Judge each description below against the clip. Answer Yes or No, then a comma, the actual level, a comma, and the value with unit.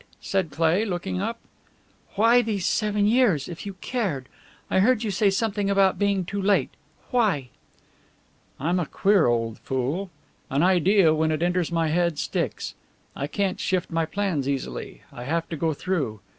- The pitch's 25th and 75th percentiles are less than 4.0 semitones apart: No, average, 4.6 semitones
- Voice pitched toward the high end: No, medium, 180 Hz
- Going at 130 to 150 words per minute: No, average, 165 wpm